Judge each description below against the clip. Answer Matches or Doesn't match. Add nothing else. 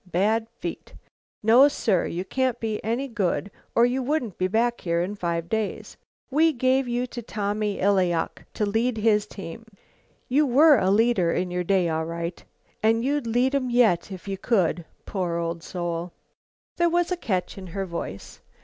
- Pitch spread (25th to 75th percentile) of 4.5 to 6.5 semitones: Matches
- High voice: Matches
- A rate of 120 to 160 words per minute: Doesn't match